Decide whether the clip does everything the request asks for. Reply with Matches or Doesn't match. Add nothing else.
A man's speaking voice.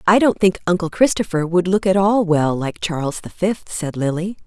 Doesn't match